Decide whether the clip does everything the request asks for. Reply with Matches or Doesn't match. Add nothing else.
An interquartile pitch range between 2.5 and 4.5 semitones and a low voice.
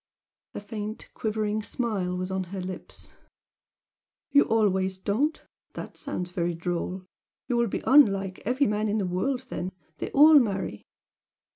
Doesn't match